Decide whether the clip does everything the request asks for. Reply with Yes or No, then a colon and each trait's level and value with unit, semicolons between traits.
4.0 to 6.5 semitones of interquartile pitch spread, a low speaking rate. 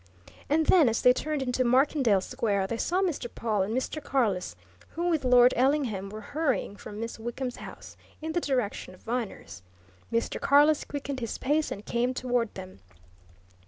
No: average, 4.7 semitones; average, 170 wpm